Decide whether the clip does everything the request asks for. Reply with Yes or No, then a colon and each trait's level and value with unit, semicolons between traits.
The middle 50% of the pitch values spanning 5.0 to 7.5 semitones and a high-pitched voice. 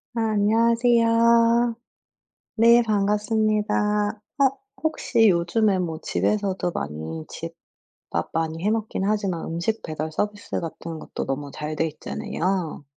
Yes: wide, 5.4 semitones; high, 205 Hz